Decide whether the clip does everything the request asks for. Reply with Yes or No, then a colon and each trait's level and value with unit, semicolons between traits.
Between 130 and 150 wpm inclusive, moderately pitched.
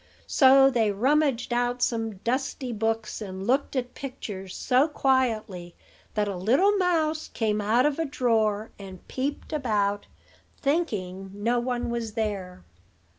No: slow, 135 wpm; high, 235 Hz